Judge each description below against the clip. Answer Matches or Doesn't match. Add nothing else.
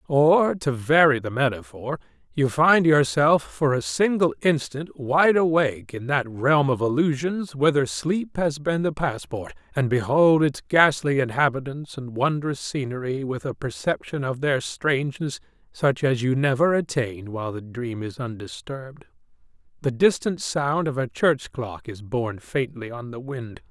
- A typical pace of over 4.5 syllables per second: Doesn't match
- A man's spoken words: Matches